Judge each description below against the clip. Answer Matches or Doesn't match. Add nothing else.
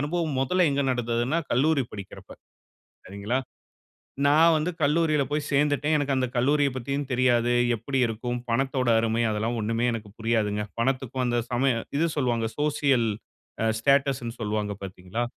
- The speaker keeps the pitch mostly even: Doesn't match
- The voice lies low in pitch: Matches